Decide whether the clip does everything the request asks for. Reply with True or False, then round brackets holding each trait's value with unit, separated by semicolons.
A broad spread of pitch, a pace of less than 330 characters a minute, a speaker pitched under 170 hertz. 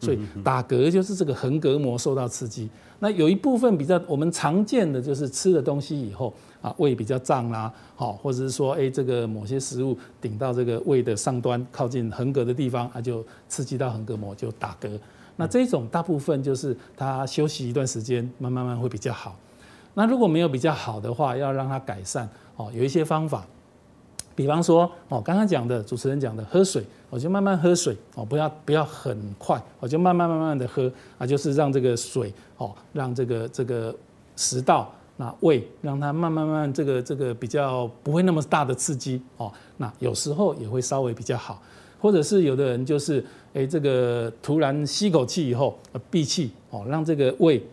False (4.0 semitones; 295 characters per minute; 135 Hz)